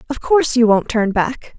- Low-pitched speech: No, high, 235 Hz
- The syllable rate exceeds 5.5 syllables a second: No, 5.0 syllables/s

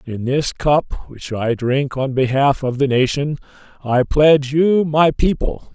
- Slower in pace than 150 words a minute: No, average, 165 wpm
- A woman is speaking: No, male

